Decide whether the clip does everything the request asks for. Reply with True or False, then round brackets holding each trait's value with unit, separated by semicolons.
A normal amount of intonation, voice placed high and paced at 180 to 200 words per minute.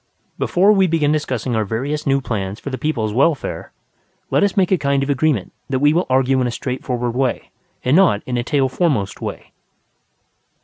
False (3.9 semitones; 135 Hz; 190 wpm)